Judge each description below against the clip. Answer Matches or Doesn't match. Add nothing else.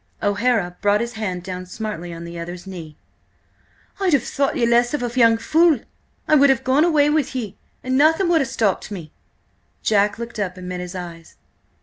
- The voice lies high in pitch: Matches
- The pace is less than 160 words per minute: Doesn't match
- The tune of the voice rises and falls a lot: Matches